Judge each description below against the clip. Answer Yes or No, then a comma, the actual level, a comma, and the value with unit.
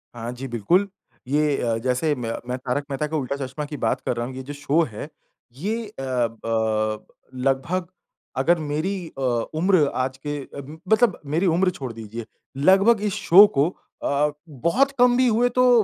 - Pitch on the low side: No, medium, 145 Hz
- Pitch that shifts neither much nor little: No, wide, 6.5 semitones